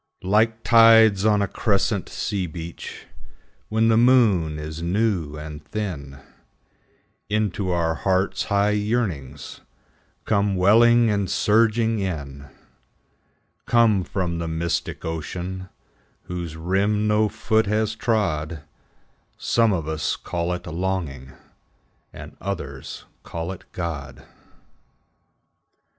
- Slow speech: Yes, slow, 105 wpm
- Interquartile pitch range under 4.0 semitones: No, average, 4.8 semitones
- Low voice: Yes, very low, 95 Hz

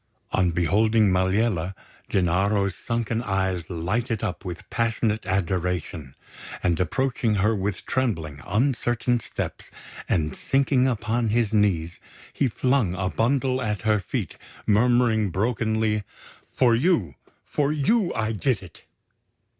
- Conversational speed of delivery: No, slow, 120 wpm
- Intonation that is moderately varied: Yes, average, 4.4 semitones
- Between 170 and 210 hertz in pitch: No, low, 105 Hz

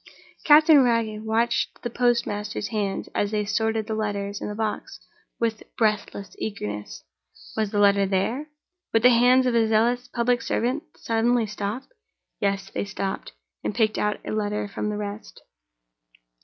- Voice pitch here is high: Yes, high, 215 Hz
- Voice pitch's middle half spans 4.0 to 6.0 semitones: No, narrow, 2.5 semitones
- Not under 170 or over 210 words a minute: No, average, 155 wpm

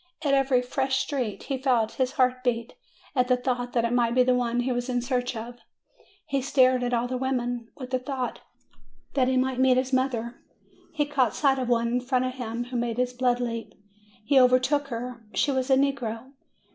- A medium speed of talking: No, fast, 210 wpm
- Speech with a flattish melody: Yes, narrow, 1.4 semitones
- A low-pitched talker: No, very high, 250 Hz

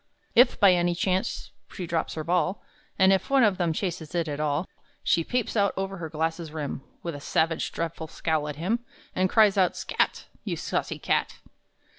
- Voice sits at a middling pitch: Yes, medium, 175 Hz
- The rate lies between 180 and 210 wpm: Yes, average, 190 wpm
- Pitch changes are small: No, average, 3.2 semitones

